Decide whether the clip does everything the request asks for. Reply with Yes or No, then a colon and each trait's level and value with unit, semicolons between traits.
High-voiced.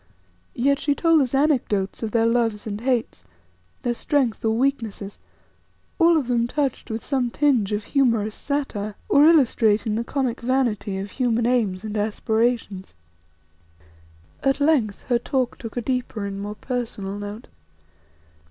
Yes: high, 235 Hz